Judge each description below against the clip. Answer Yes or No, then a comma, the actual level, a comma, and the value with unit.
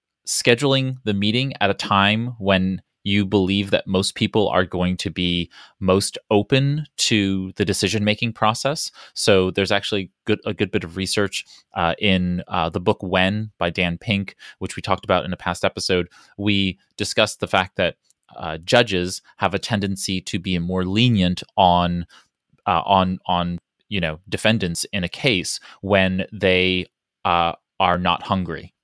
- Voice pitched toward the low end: Yes, very low, 95 Hz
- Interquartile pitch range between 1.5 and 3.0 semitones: Yes, narrow, 2.6 semitones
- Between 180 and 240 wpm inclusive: No, average, 160 wpm